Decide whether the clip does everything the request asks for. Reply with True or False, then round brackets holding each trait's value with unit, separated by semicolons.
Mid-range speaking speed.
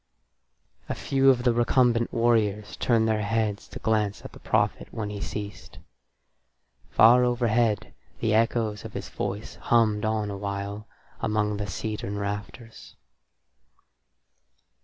False (125 wpm)